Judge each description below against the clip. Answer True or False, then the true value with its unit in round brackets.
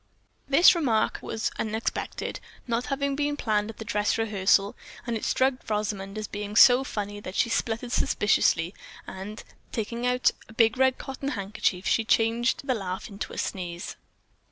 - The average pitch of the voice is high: True (220 Hz)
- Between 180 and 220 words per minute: False (160 wpm)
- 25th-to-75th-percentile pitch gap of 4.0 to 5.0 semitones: False (3.3 semitones)